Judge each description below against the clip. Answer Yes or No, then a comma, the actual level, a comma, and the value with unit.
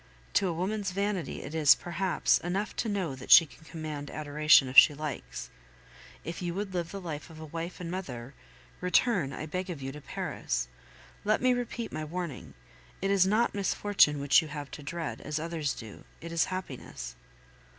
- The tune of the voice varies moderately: Yes, average, 4.2 semitones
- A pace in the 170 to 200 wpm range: Yes, average, 190 wpm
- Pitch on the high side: No, medium, 165 Hz